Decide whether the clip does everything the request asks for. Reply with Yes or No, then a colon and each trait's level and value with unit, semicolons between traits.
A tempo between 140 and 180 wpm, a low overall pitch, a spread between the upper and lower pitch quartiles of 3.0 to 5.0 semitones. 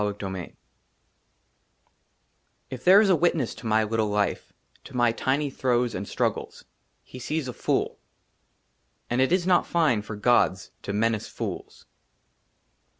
No: average, 150 wpm; low, 120 Hz; wide, 5.5 semitones